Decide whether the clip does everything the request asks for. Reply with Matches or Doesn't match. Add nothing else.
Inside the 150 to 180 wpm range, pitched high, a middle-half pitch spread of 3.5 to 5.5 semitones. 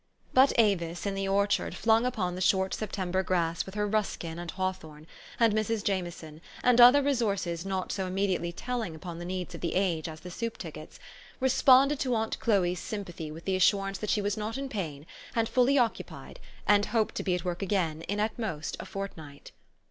Doesn't match